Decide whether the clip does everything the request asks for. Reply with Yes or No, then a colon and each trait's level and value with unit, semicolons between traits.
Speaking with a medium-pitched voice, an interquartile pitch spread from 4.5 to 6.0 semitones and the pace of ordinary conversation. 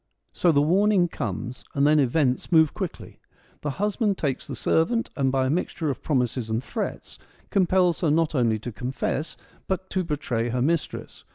Yes: medium, 150 Hz; wide, 5.5 semitones; average, 175 wpm